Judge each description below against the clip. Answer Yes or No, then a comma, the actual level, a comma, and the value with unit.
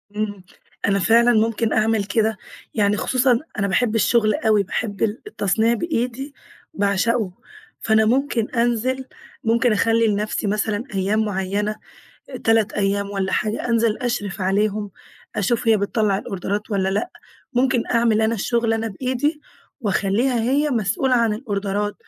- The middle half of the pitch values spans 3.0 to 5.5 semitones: No, narrow, 2.6 semitones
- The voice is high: Yes, high, 220 Hz